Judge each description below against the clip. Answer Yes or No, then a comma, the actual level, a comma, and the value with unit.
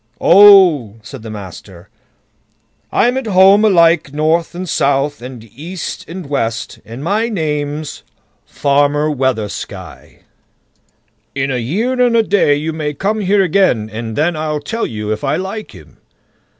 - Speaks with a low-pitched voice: No, medium, 150 Hz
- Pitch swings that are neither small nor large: No, wide, 6.9 semitones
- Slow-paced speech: No, average, 145 wpm